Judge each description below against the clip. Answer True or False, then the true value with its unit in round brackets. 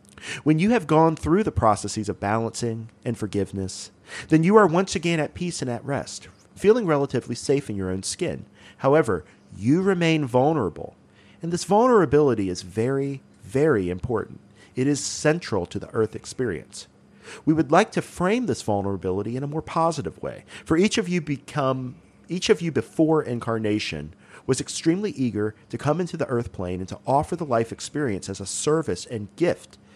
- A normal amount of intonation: False (7.5 semitones)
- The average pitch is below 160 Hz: True (135 Hz)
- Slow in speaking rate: False (175 wpm)